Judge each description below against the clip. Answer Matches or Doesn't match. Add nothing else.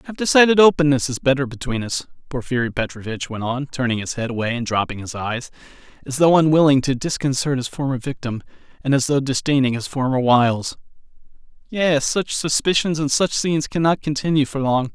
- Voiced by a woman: Doesn't match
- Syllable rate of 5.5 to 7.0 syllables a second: Matches